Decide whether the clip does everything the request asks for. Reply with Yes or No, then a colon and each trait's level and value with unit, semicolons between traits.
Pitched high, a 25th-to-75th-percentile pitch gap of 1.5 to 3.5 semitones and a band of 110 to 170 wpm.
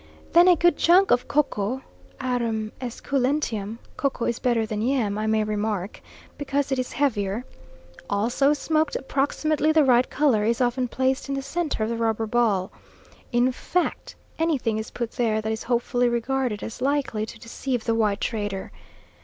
No: high, 245 Hz; average, 4.0 semitones; average, 165 wpm